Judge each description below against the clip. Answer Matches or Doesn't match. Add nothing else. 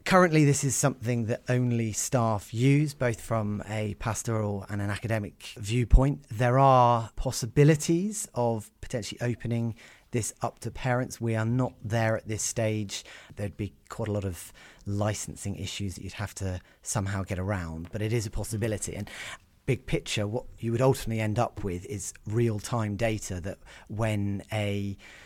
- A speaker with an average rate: Matches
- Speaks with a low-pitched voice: Matches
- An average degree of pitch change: Matches